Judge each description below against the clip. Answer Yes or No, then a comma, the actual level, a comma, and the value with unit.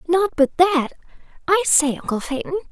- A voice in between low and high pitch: No, very high, 330 Hz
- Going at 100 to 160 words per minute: Yes, slow, 135 wpm